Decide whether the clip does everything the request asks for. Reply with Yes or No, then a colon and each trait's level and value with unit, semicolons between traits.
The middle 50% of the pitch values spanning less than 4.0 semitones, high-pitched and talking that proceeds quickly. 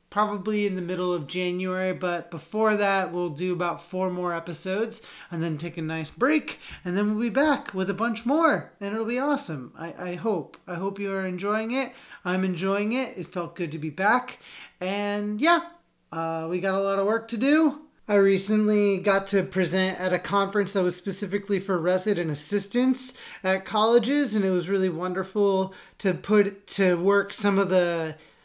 No: average, 2.8 semitones; high, 195 Hz; average, 190 wpm